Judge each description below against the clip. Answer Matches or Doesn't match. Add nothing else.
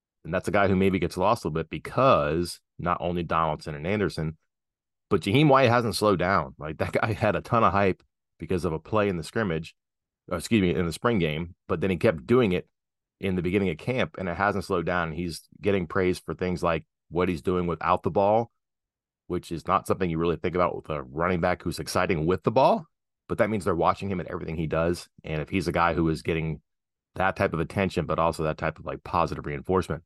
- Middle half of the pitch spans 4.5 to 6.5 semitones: Doesn't match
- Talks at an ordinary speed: Doesn't match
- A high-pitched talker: Doesn't match